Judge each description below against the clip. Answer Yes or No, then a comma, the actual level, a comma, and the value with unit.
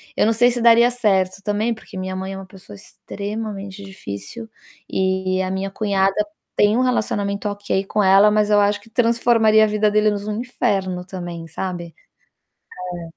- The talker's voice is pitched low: No, high, 205 Hz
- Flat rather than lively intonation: Yes, narrow, 2.3 semitones